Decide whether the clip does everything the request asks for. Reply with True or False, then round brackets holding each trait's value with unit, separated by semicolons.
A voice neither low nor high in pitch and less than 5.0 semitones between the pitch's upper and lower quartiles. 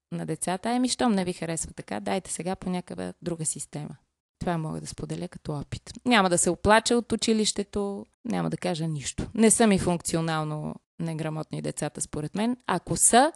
False (175 Hz; 5.3 semitones)